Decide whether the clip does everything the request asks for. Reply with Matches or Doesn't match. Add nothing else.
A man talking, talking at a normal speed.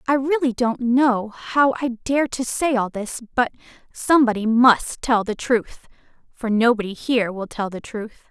Doesn't match